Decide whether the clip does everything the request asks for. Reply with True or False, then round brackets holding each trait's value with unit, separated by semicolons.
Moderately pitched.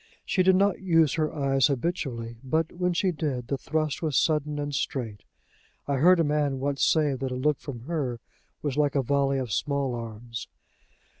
True (145 Hz)